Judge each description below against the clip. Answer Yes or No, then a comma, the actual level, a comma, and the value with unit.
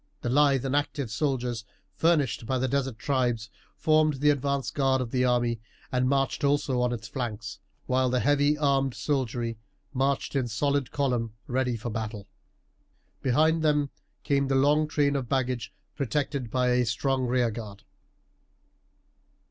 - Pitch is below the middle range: Yes, low, 130 Hz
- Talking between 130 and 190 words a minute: Yes, average, 150 wpm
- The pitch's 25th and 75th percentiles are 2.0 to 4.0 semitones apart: Yes, average, 2.7 semitones